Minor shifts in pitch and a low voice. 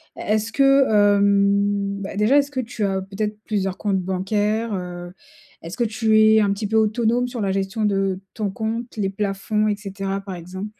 No: narrow, 2.0 semitones; high, 205 Hz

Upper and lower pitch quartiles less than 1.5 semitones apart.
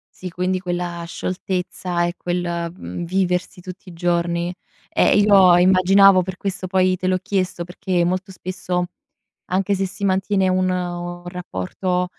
Yes: narrow, 1.1 semitones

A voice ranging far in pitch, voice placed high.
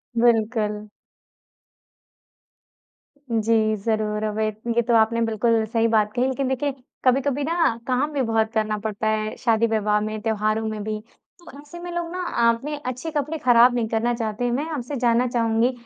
No: average, 2.8 semitones; high, 230 Hz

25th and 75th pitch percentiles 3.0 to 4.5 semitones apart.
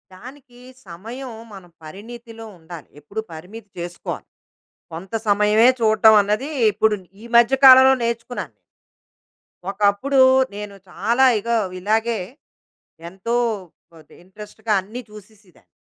Yes: average, 3.3 semitones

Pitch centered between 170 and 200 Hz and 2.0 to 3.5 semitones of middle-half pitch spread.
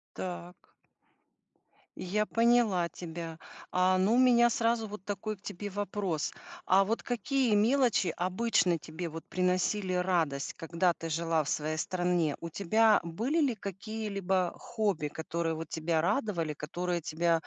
No: medium, 185 Hz; average, 4.2 semitones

